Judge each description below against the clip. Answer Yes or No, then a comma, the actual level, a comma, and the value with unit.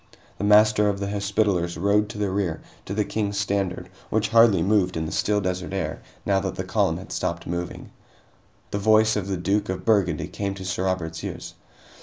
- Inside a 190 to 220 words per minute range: Yes, average, 200 wpm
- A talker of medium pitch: No, low, 100 Hz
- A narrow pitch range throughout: Yes, narrow, 2.3 semitones